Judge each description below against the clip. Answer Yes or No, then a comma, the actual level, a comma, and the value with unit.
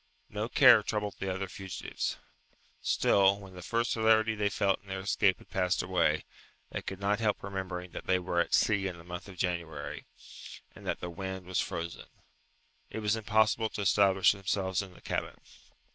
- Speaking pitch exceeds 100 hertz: No, very low, 95 Hz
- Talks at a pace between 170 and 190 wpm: Yes, average, 185 wpm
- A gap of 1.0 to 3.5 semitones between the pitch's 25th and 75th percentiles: Yes, narrow, 2.4 semitones